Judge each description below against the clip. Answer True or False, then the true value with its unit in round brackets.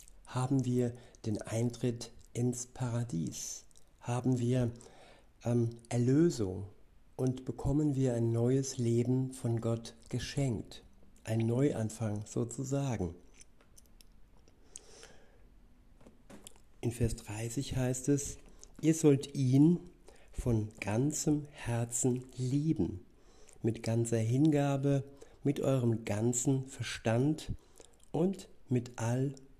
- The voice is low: True (125 Hz)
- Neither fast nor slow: False (90 wpm)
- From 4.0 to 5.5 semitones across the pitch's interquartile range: False (2.9 semitones)